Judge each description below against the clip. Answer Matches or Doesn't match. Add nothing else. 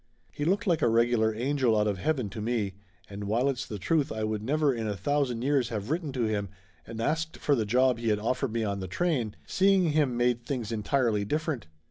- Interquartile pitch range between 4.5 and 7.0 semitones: Matches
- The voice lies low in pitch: Matches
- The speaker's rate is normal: Doesn't match